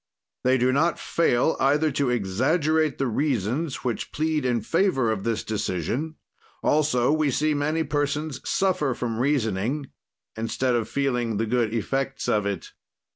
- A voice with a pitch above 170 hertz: No, low, 130 Hz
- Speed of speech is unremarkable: Yes, average, 145 wpm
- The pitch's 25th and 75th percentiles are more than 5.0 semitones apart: No, average, 4.6 semitones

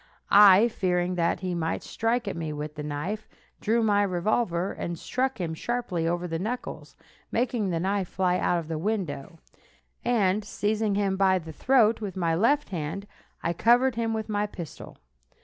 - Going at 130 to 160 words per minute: No, average, 175 wpm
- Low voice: No, high, 190 Hz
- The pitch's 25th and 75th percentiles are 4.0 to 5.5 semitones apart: Yes, average, 4.5 semitones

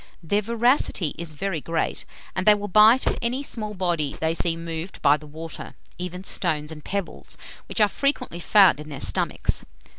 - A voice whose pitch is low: No, medium, 175 Hz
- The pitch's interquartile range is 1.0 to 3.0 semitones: No, average, 4.7 semitones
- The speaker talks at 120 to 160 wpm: No, average, 180 wpm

